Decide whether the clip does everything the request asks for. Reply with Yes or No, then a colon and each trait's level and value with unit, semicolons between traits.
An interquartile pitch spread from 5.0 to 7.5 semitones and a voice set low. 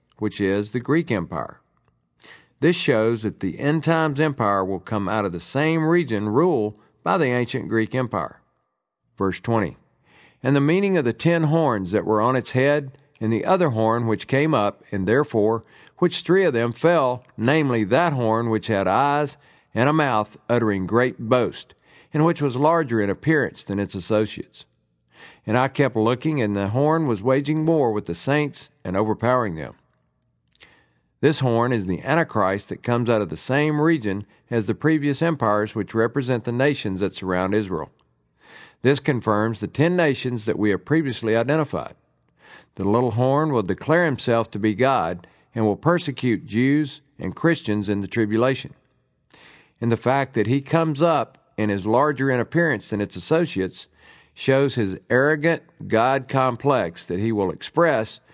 Yes: wide, 5.5 semitones; low, 120 Hz